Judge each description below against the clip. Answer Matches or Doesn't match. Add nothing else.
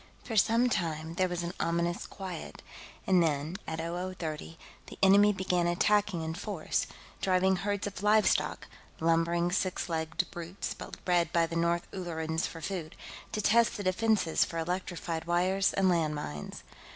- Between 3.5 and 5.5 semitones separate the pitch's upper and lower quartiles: Doesn't match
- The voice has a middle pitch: Matches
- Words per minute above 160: Doesn't match